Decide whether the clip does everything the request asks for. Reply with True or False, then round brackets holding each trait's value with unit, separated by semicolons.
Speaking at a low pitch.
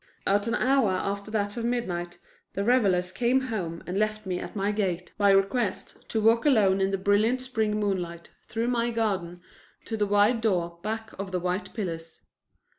False (205 Hz)